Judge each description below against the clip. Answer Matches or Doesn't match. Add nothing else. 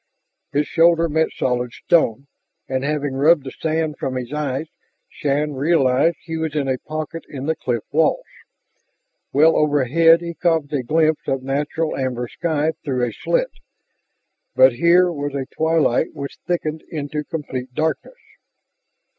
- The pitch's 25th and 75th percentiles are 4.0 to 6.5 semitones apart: Doesn't match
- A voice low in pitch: Doesn't match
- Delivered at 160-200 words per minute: Doesn't match